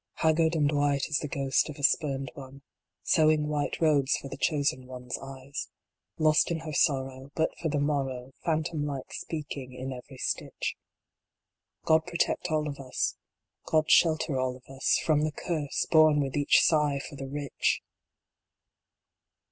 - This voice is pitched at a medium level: Yes, medium, 145 Hz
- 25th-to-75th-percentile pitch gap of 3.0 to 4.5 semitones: No, narrow, 2.5 semitones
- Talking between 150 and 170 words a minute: Yes, average, 165 wpm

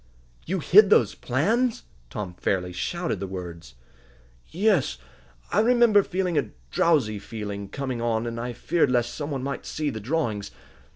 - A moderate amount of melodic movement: No, wide, 8.8 semitones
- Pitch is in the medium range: No, low, 125 Hz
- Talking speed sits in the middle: Yes, average, 155 wpm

